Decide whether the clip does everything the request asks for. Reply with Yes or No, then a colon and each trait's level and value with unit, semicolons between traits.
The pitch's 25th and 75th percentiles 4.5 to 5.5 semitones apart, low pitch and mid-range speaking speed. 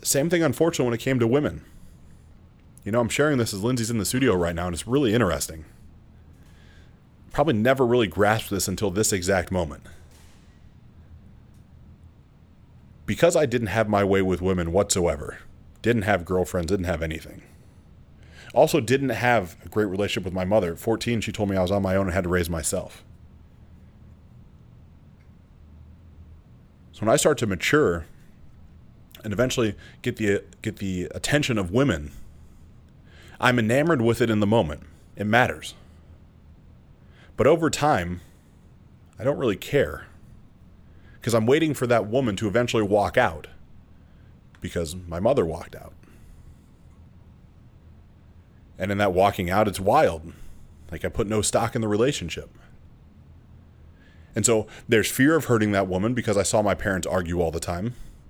Yes: average, 4.8 semitones; low, 100 Hz; average, 155 wpm